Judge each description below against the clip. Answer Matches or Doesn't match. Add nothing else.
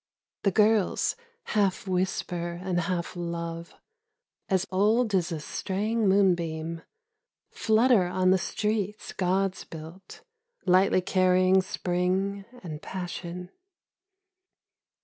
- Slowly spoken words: Matches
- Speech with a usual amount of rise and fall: Doesn't match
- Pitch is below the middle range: Doesn't match